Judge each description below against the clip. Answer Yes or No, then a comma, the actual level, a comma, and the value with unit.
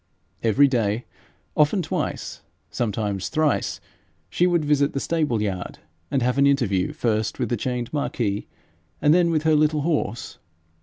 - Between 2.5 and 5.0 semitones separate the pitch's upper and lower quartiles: No, wide, 5.5 semitones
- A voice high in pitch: No, low, 135 Hz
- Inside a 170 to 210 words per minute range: No, average, 150 wpm